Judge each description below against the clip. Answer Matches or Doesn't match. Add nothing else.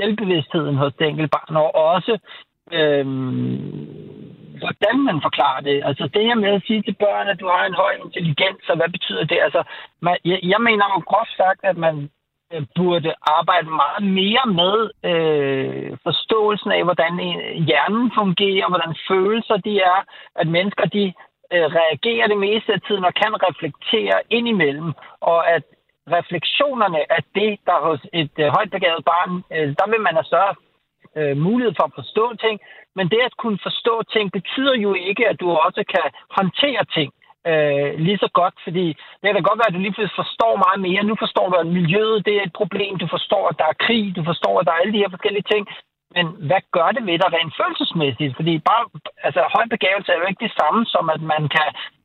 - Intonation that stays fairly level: Doesn't match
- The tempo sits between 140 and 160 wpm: Doesn't match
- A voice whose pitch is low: Doesn't match